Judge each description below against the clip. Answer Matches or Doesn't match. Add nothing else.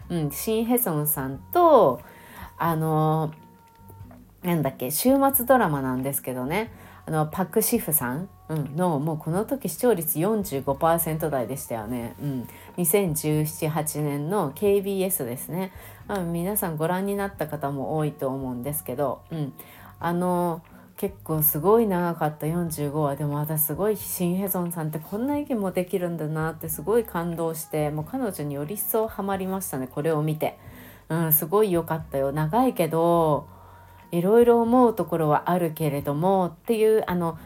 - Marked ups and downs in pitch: Doesn't match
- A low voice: Doesn't match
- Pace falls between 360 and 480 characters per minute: Doesn't match